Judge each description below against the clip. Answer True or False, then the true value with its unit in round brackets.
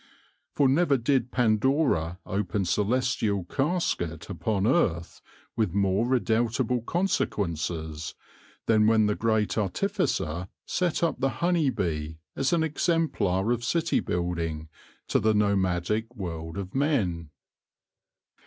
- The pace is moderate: False (115 wpm)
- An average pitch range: False (7.1 semitones)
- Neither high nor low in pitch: False (110 Hz)